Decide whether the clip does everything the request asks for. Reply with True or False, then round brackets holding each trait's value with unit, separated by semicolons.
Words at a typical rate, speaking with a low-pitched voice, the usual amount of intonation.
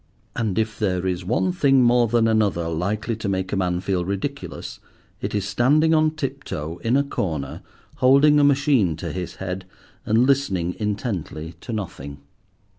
False (170 wpm; 105 Hz; 6.6 semitones)